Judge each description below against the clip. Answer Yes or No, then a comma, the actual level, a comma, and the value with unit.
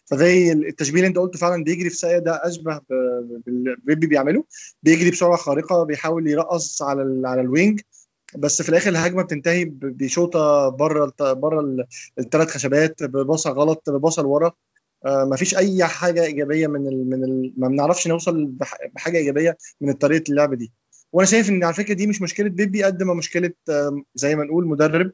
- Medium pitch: Yes, medium, 160 Hz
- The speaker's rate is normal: No, fast, 165 wpm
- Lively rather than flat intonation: No, average, 3.6 semitones